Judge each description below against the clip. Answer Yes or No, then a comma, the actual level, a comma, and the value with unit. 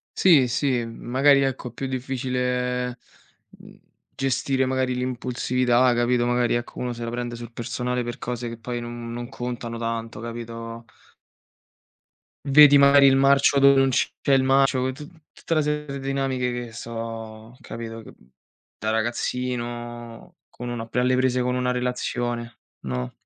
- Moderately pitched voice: No, low, 125 Hz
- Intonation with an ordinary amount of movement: No, narrow, 1.9 semitones